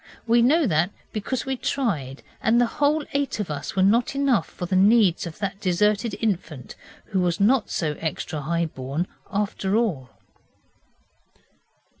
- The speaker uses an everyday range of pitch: No, wide, 5.8 semitones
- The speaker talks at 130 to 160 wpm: Yes, average, 155 wpm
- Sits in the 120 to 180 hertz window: No, high, 200 Hz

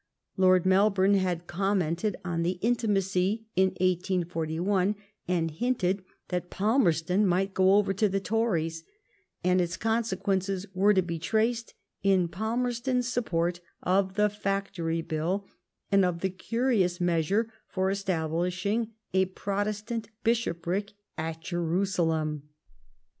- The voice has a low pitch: No, high, 190 Hz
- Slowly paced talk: Yes, slow, 120 wpm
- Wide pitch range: No, average, 3.0 semitones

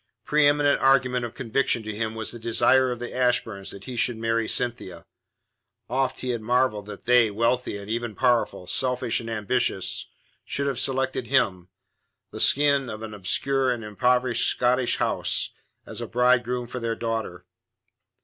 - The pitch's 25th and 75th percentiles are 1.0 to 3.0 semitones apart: Yes, narrow, 2.4 semitones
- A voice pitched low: Yes, low, 120 Hz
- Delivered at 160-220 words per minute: Yes, average, 165 wpm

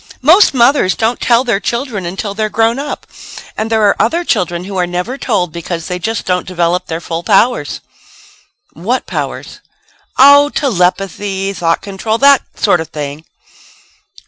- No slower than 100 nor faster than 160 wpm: Yes, average, 155 wpm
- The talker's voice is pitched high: Yes, high, 200 Hz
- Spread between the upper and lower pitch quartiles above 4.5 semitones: Yes, average, 5.0 semitones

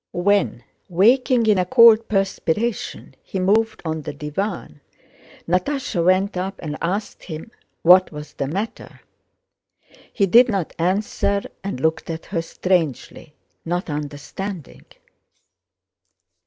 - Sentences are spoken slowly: Yes, slow, 115 wpm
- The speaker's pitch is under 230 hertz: Yes, medium, 185 Hz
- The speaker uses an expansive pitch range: No, average, 4.3 semitones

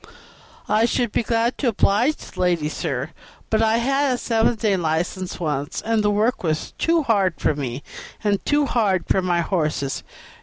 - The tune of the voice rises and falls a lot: Yes, wide, 5.7 semitones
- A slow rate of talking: No, average, 180 wpm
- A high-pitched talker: Yes, high, 205 Hz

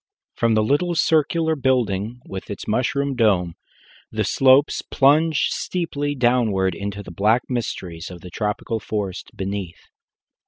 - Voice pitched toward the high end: No, low, 115 Hz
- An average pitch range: No, wide, 6.0 semitones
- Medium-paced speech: No, slow, 130 wpm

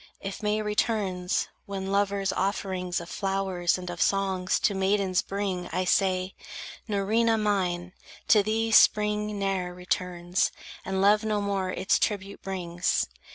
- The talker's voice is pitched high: Yes, high, 195 Hz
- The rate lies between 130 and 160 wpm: Yes, slow, 135 wpm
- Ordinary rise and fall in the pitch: No, narrow, 2.1 semitones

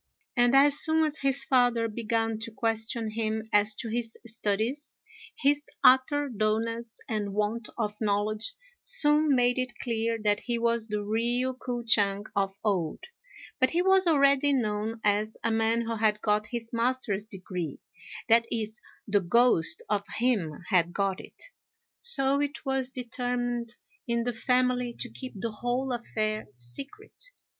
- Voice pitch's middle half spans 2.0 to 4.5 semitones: Yes, average, 3.2 semitones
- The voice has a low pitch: No, high, 230 Hz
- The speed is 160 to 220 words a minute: No, average, 150 wpm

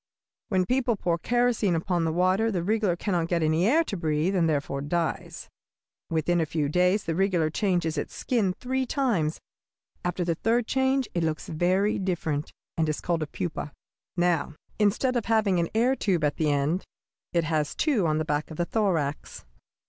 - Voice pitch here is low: No, medium, 175 Hz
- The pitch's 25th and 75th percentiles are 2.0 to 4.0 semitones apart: No, average, 4.8 semitones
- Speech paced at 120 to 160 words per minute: No, average, 185 wpm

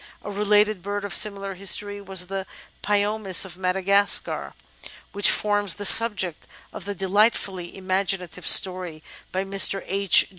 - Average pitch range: No, narrow, 1.6 semitones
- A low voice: No, high, 195 Hz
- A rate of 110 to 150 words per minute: Yes, average, 140 wpm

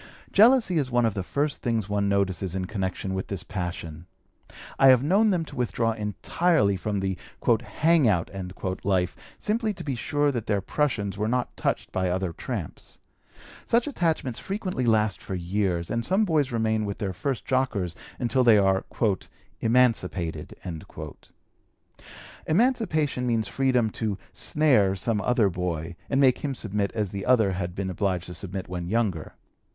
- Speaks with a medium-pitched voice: No, low, 110 Hz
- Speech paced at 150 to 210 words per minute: Yes, average, 160 wpm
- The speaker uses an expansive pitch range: Yes, wide, 5.9 semitones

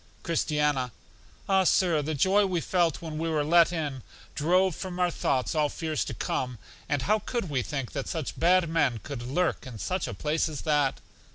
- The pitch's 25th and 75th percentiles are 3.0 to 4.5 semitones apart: Yes, average, 3.7 semitones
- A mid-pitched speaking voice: Yes, medium, 155 Hz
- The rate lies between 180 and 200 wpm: Yes, average, 195 wpm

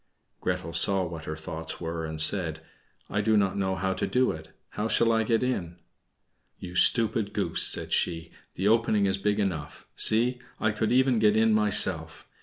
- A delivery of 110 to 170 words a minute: No, average, 185 wpm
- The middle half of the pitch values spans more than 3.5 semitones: Yes, average, 4.9 semitones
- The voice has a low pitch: Yes, low, 100 Hz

